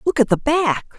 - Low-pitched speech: No, very high, 265 Hz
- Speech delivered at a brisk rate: Yes, fast, 245 wpm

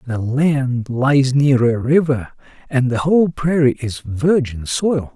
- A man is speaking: Yes, male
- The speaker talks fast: No, average, 150 wpm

